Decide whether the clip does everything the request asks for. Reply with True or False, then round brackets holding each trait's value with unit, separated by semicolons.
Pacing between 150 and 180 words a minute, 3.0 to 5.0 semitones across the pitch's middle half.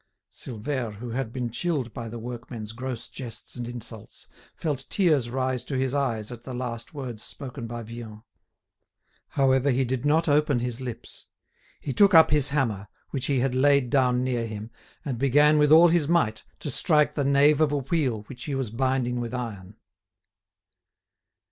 True (175 wpm; 3.3 semitones)